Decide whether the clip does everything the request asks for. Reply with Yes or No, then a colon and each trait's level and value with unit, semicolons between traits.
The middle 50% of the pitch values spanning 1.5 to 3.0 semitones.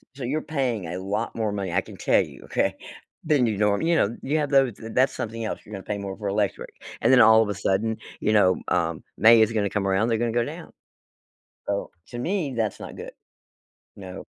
No: average, 3.6 semitones